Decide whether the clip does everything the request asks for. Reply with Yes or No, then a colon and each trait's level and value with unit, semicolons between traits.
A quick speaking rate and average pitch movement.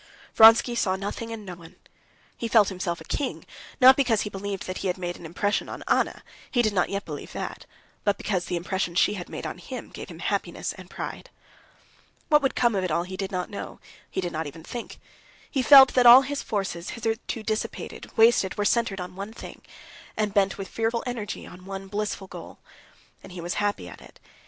Yes: fast, 210 wpm; average, 3.7 semitones